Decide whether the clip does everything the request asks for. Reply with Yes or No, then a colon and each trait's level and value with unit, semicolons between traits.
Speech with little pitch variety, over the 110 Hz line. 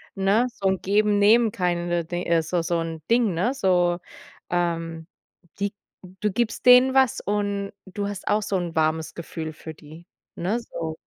No: average, 3.8 semitones; medium, 185 Hz